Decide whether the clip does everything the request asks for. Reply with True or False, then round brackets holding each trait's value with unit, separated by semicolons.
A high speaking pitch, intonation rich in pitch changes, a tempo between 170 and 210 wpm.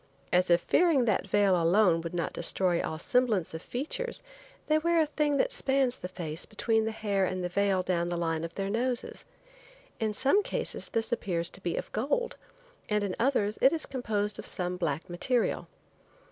True (205 Hz; 6.3 semitones; 195 wpm)